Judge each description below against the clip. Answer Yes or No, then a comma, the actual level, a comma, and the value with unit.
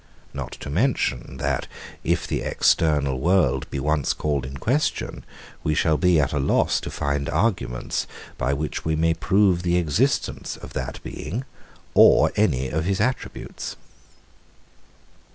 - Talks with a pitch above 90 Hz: No, very low, 75 Hz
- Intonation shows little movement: No, average, 4.5 semitones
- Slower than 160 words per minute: Yes, average, 145 wpm